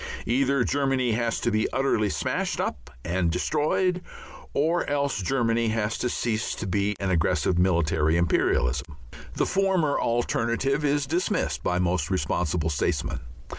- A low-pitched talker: Yes, low, 110 Hz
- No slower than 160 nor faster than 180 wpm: No, slow, 135 wpm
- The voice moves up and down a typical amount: No, wide, 7.6 semitones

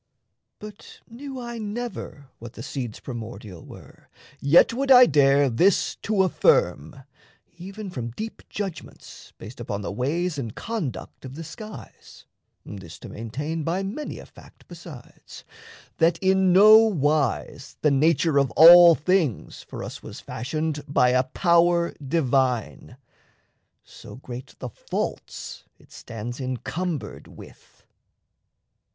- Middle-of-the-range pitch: Yes, medium, 155 Hz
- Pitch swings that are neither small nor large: No, wide, 6.9 semitones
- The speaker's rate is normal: No, slow, 130 wpm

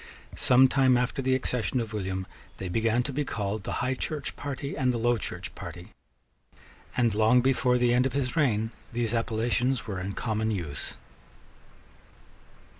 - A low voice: Yes, low, 120 Hz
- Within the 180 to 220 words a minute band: No, average, 165 wpm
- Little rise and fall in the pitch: No, average, 3.0 semitones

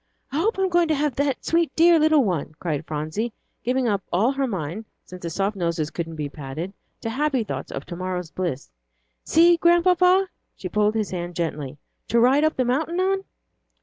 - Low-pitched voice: No, high, 220 Hz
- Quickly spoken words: No, average, 195 wpm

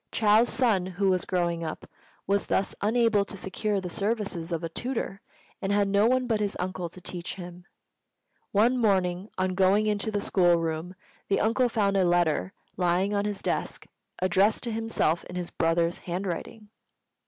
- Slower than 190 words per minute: Yes, average, 175 wpm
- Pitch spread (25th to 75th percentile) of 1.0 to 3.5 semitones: Yes, average, 3.1 semitones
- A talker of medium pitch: No, high, 195 Hz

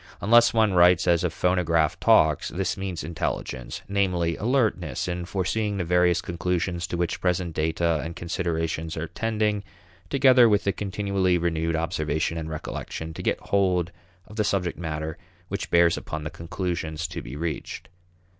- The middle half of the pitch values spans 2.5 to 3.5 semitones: Yes, average, 2.9 semitones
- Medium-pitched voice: No, very low, 85 Hz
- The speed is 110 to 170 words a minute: Yes, average, 155 wpm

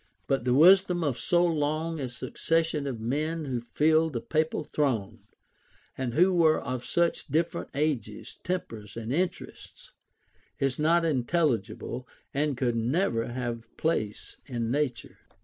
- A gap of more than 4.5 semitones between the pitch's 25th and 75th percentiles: Yes, average, 5.2 semitones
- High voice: No, medium, 145 Hz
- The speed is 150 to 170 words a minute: No, slow, 135 wpm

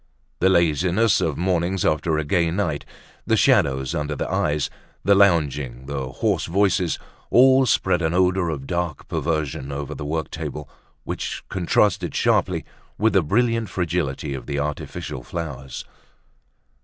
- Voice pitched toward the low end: Yes, very low, 80 Hz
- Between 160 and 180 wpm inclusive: No, average, 145 wpm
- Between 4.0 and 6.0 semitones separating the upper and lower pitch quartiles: Yes, average, 4.3 semitones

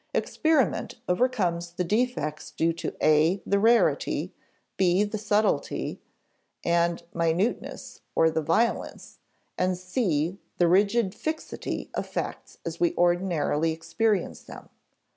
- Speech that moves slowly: Yes, slow, 115 wpm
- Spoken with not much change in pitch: No, average, 4.1 semitones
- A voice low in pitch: No, medium, 180 Hz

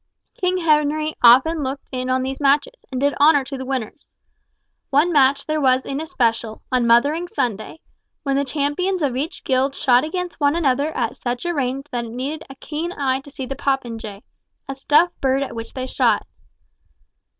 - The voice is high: Yes, very high, 275 Hz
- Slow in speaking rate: No, average, 185 wpm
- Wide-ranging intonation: No, average, 3.0 semitones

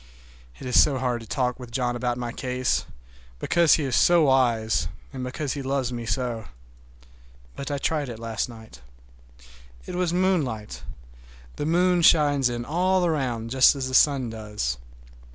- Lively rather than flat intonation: No, average, 3.8 semitones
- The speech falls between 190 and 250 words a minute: No, average, 165 wpm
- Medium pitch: No, low, 130 Hz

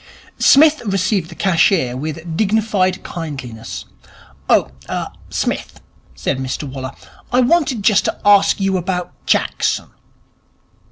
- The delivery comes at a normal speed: No, slow, 120 wpm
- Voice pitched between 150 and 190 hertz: Yes, medium, 185 Hz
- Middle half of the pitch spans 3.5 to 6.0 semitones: Yes, wide, 5.6 semitones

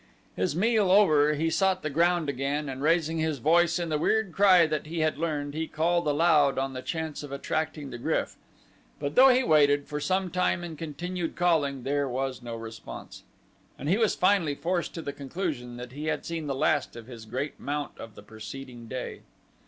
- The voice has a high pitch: No, medium, 150 Hz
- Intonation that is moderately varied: Yes, average, 3.9 semitones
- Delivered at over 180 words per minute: Yes, average, 200 wpm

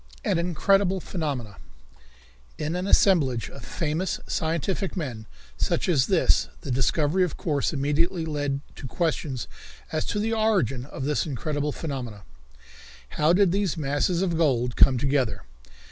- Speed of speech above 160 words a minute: No, average, 140 wpm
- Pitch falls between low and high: Yes, medium, 150 Hz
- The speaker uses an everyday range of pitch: Yes, average, 4.7 semitones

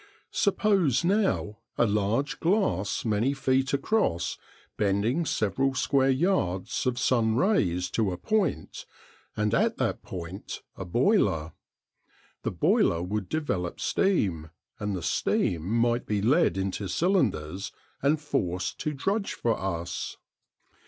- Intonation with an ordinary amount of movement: No, wide, 7.6 semitones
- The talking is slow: Yes, slow, 125 wpm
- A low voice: Yes, low, 115 Hz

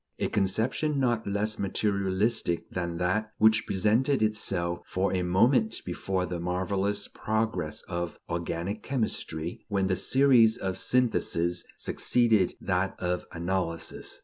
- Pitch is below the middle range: Yes, low, 100 Hz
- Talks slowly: Yes, slow, 120 wpm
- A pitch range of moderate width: Yes, average, 3.6 semitones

